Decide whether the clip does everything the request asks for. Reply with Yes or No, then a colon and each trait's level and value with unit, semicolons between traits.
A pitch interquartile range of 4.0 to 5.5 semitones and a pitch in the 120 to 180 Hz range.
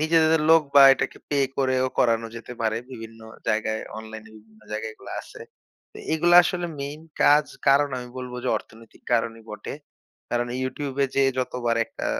Yes: average, 4.3 semitones; low, 125 Hz